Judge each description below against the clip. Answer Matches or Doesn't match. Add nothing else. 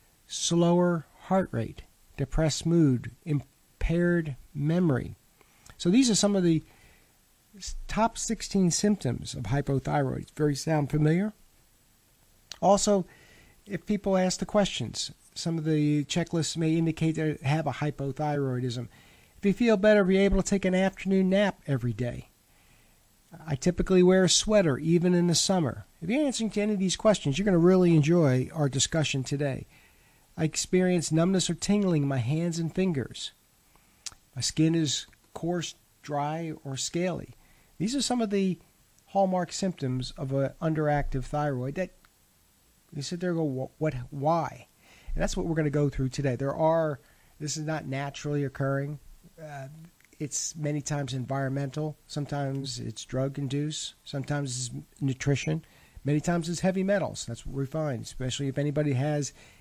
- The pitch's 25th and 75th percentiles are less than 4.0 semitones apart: Doesn't match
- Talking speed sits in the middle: Matches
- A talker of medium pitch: Matches